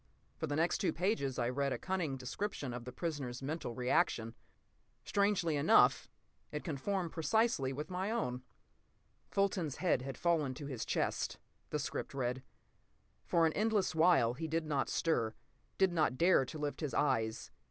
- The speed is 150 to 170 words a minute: Yes, average, 165 wpm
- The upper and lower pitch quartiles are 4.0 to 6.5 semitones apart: Yes, average, 5.2 semitones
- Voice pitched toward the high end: No, medium, 150 Hz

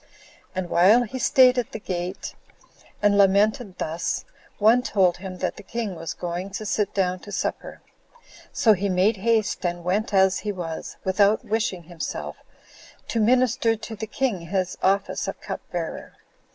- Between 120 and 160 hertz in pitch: No, high, 200 Hz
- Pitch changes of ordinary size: Yes, average, 3.3 semitones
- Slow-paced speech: No, average, 165 wpm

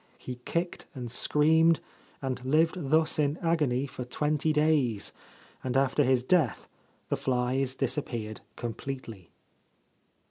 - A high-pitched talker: No, low, 135 Hz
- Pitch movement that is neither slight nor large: Yes, average, 3.7 semitones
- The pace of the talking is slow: Yes, slow, 115 wpm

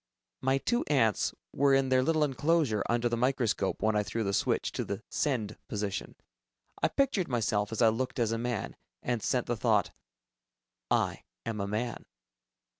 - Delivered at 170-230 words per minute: Yes, average, 175 wpm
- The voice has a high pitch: No, low, 120 Hz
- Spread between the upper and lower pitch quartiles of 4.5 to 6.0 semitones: No, average, 3.7 semitones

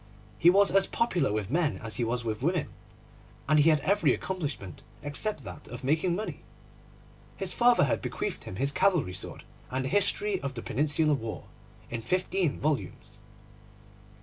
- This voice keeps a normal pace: Yes, average, 165 wpm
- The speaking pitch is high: No, medium, 150 Hz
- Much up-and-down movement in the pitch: Yes, wide, 6.9 semitones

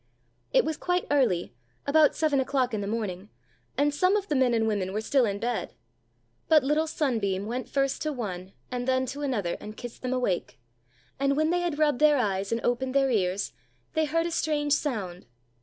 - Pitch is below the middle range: No, very high, 260 Hz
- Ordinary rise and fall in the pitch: No, wide, 5.7 semitones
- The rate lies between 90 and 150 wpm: No, average, 200 wpm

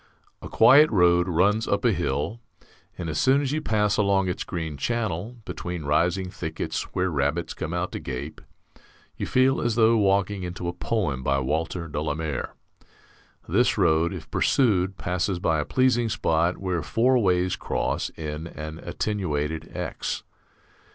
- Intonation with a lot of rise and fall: No, average, 4.8 semitones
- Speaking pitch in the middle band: No, very low, 90 Hz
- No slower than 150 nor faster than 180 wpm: Yes, average, 160 wpm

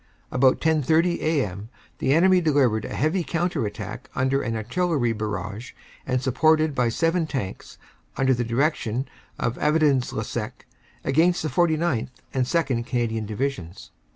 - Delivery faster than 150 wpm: No, average, 140 wpm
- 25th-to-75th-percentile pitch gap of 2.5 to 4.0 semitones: No, wide, 5.4 semitones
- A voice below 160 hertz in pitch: Yes, low, 135 Hz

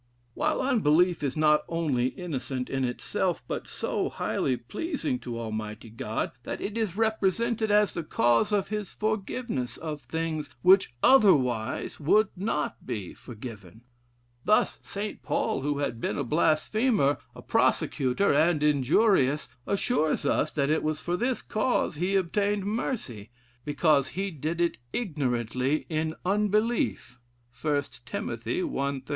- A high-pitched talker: No, medium, 155 Hz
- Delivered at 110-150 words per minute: Yes, average, 140 wpm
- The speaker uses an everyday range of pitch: No, wide, 7.6 semitones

